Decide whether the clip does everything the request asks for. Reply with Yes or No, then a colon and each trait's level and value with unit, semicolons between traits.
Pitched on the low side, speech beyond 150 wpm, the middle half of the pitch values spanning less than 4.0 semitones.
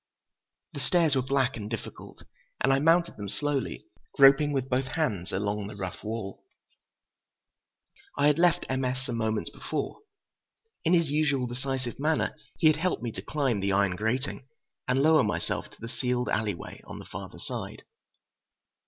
No: low, 130 Hz; average, 170 wpm; average, 5.0 semitones